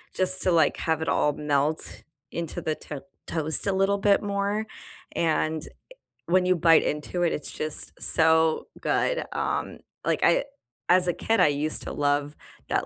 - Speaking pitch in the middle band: Yes, medium, 160 Hz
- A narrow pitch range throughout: No, average, 3.4 semitones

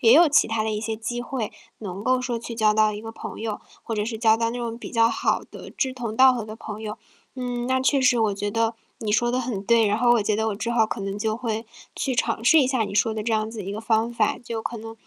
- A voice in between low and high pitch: No, high, 225 Hz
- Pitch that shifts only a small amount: Yes, narrow, 2.0 semitones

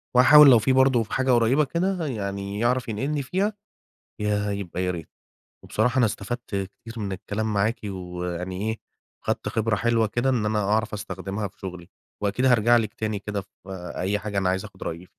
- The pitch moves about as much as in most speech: Yes, average, 3.5 semitones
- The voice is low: Yes, low, 105 Hz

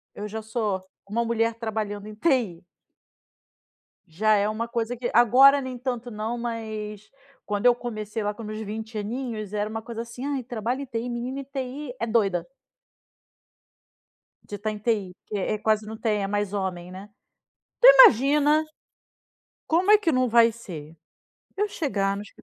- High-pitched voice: Yes, high, 225 Hz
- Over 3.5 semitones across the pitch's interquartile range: No, average, 2.8 semitones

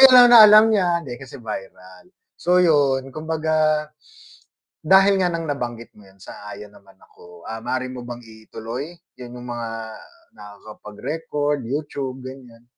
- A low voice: Yes, low, 130 Hz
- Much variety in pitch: Yes, wide, 5.8 semitones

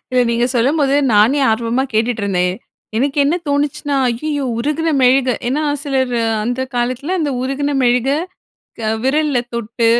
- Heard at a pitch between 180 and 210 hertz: No, very high, 260 Hz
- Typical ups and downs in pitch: Yes, average, 3.3 semitones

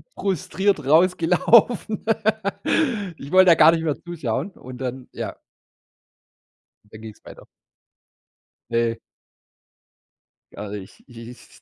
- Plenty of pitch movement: Yes, wide, 7.5 semitones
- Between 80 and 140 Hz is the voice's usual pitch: No, medium, 150 Hz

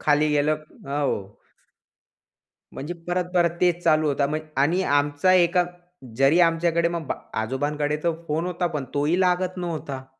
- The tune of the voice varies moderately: Yes, average, 3.1 semitones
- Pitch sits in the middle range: Yes, medium, 155 Hz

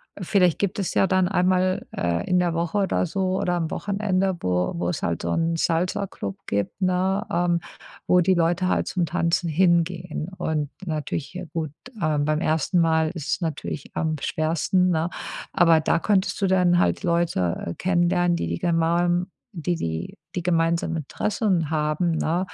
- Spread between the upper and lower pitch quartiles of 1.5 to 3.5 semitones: Yes, narrow, 2.5 semitones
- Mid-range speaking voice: Yes, medium, 170 Hz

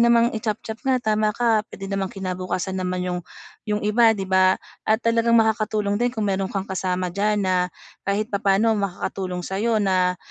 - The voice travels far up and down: No, average, 2.7 semitones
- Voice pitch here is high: Yes, high, 200 Hz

